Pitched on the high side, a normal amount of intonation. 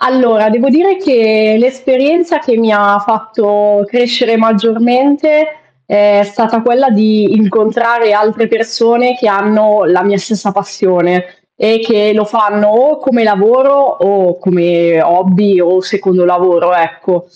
Yes: high, 215 Hz; average, 3.2 semitones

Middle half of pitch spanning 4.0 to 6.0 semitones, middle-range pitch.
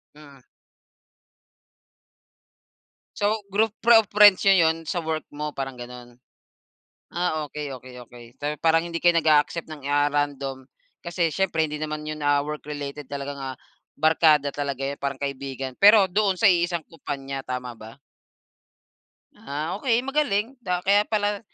Yes: average, 4.4 semitones; medium, 150 Hz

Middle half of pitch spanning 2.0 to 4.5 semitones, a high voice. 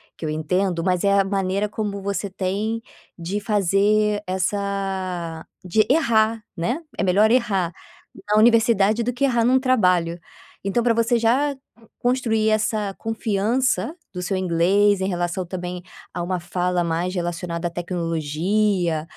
Yes: average, 3.6 semitones; high, 195 Hz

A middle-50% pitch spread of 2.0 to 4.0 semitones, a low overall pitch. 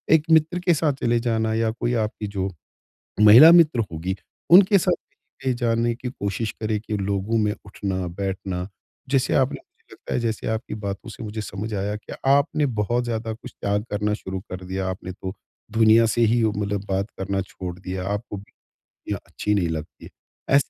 Yes: average, 3.4 semitones; low, 105 Hz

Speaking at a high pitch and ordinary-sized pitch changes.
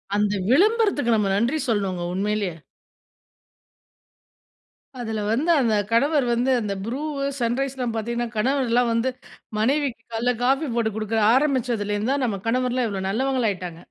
Yes: high, 235 Hz; average, 3.7 semitones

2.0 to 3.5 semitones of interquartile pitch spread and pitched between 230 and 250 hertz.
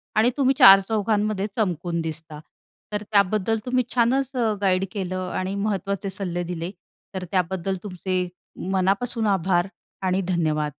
No: average, 2.8 semitones; high, 190 Hz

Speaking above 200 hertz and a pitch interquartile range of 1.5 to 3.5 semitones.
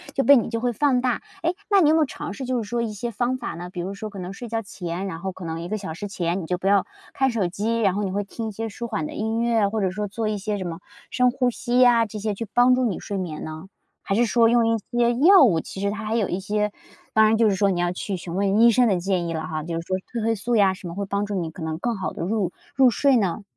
No: high, 210 Hz; average, 3.9 semitones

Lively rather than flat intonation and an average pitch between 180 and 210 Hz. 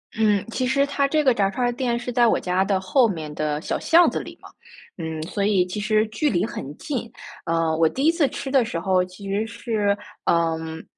Yes: wide, 6.2 semitones; high, 205 Hz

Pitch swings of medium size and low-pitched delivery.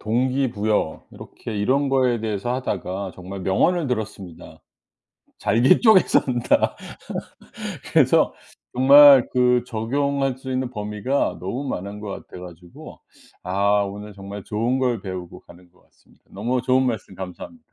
Yes: average, 4.8 semitones; low, 110 Hz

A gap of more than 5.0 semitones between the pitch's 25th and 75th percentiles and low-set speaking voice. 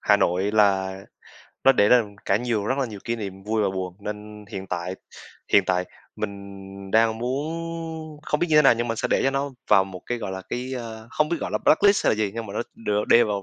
No: average, 3.7 semitones; low, 110 Hz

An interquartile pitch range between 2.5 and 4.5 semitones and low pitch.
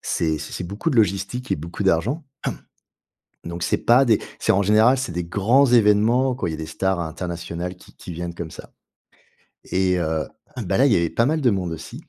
No: wide, 5.5 semitones; very low, 95 Hz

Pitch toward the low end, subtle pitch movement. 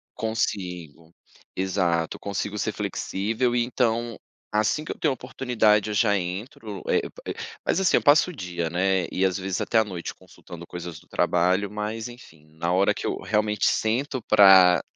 No: low, 100 Hz; average, 4.1 semitones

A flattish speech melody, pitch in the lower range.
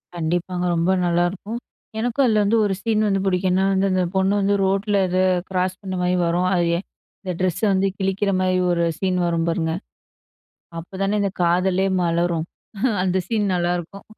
No: narrow, 2.0 semitones; medium, 185 Hz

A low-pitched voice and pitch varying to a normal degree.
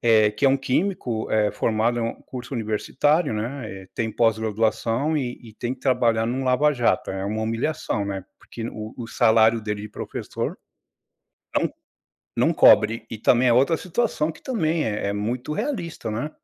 Yes: low, 115 Hz; average, 3.8 semitones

